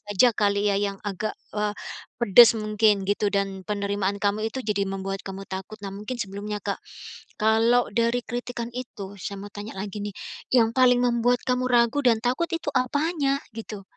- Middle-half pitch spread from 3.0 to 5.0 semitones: Yes, average, 3.3 semitones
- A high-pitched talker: Yes, high, 215 Hz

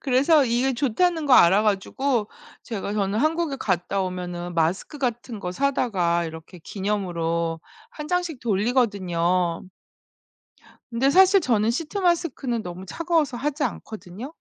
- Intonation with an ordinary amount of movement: No, wide, 7.5 semitones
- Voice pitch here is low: No, high, 225 Hz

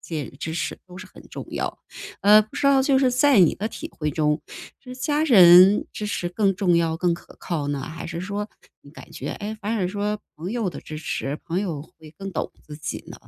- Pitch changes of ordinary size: Yes, average, 4.6 semitones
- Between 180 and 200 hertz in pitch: Yes, medium, 185 Hz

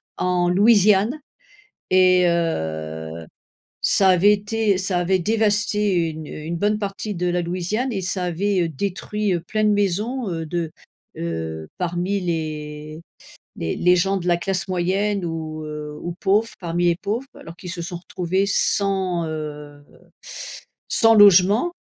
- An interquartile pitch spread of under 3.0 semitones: No, average, 3.5 semitones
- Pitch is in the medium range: Yes, medium, 180 Hz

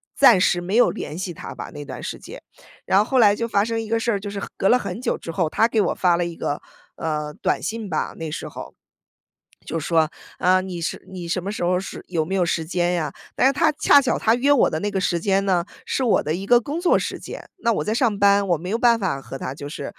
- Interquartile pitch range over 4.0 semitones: Yes, average, 4.9 semitones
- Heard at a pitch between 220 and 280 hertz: No, high, 190 Hz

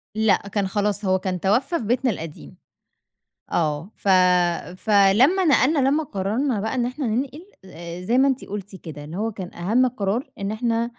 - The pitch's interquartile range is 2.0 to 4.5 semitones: No, average, 4.9 semitones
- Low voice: No, high, 210 Hz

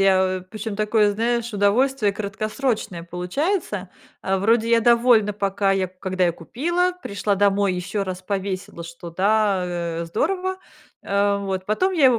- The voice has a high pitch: Yes, high, 200 Hz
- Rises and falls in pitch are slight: No, average, 3.6 semitones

